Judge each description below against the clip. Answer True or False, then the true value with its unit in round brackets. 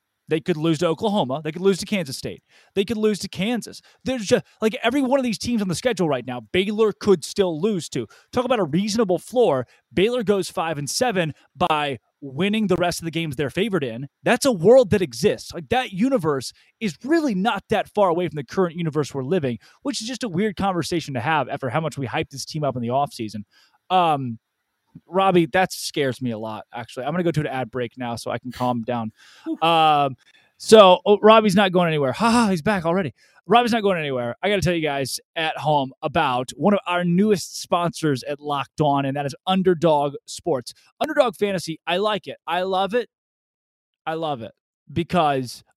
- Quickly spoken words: True (215 wpm)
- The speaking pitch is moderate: True (170 Hz)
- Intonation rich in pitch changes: True (6.6 semitones)